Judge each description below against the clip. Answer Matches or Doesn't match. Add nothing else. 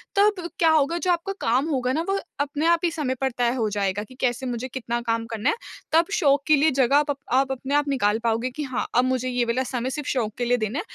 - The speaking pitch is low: Doesn't match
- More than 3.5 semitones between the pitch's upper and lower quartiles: Matches